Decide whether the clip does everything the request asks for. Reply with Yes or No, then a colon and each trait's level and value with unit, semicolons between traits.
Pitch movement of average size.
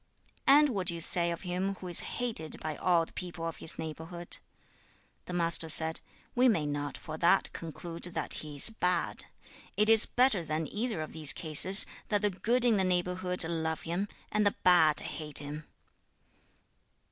Yes: average, 3.6 semitones